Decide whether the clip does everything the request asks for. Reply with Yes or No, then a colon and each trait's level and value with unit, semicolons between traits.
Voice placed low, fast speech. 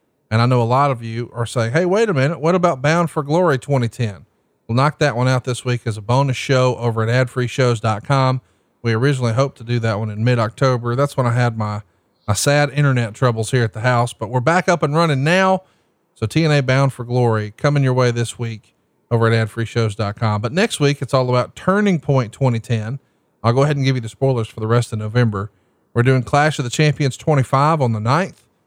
Yes: low, 125 Hz; fast, 225 wpm